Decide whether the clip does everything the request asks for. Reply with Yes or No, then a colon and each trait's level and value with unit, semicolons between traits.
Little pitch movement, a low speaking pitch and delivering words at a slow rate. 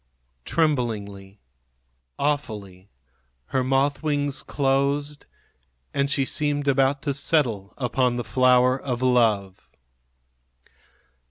No: average, 3.2 semitones; low, 130 Hz; slow, 90 wpm